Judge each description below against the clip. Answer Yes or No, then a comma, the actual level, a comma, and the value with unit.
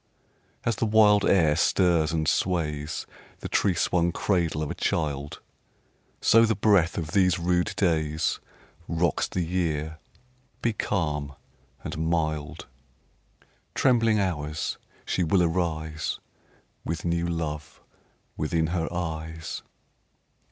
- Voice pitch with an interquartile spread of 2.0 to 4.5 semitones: Yes, average, 2.8 semitones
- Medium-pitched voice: No, very low, 85 Hz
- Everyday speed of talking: No, slow, 120 wpm